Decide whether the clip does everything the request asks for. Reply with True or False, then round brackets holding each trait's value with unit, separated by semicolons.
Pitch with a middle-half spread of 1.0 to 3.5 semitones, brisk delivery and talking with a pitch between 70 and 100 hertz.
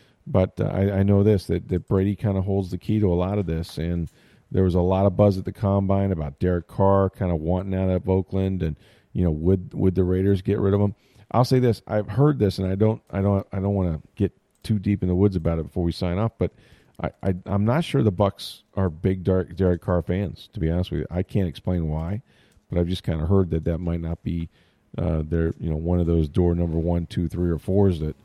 True (2.6 semitones; 265 wpm; 95 Hz)